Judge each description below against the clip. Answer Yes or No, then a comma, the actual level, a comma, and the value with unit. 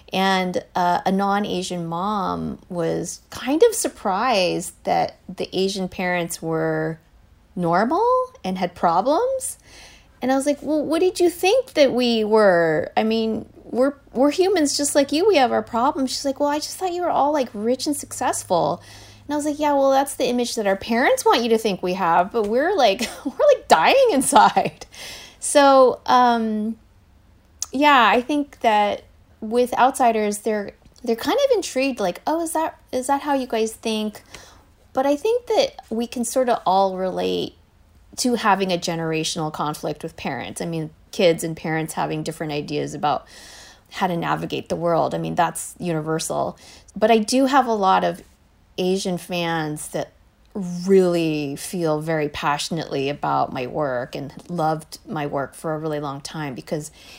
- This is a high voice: Yes, high, 210 Hz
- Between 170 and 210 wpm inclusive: Yes, average, 175 wpm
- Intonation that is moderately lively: No, wide, 8.6 semitones